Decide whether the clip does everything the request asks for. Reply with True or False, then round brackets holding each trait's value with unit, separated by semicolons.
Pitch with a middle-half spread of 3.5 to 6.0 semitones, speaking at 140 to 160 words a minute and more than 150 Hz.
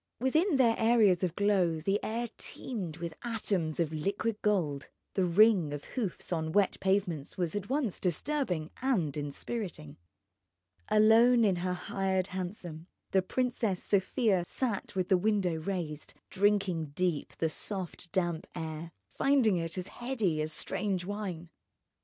True (4.2 semitones; 145 wpm; 190 Hz)